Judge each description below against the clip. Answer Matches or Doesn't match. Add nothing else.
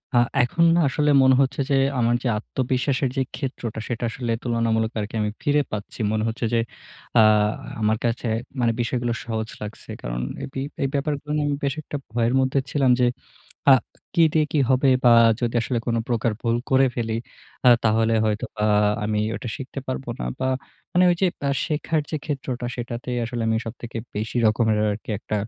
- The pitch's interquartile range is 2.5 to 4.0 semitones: Matches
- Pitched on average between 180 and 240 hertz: Doesn't match